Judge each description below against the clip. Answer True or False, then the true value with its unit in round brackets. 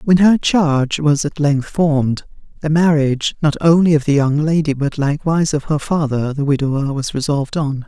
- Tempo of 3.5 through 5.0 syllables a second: False (5.3 syllables/s)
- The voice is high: False (150 Hz)